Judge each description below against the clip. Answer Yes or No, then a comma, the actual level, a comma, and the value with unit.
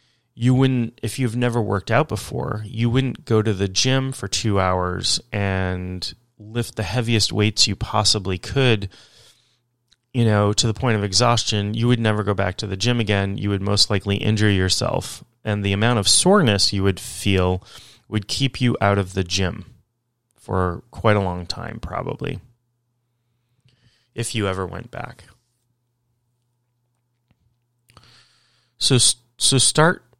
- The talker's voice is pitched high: No, low, 115 Hz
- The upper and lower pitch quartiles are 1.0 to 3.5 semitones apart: Yes, average, 3.2 semitones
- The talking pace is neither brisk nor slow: Yes, average, 150 wpm